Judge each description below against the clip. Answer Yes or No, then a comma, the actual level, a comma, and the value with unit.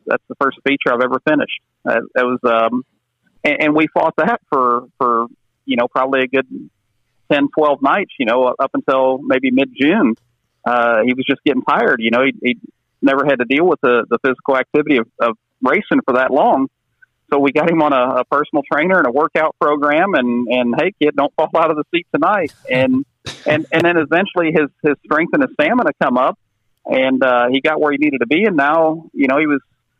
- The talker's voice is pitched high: No, low, 135 Hz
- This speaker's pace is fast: Yes, fast, 220 wpm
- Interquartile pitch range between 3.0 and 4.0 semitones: Yes, average, 3.5 semitones